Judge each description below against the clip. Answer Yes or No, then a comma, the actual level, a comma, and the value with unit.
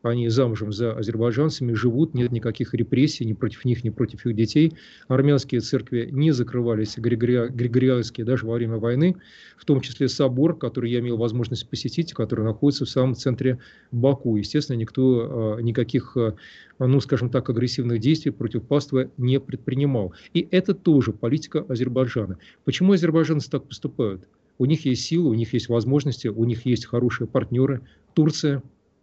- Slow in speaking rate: No, average, 155 wpm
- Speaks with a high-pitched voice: No, low, 125 Hz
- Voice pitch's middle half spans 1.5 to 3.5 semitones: Yes, average, 2.8 semitones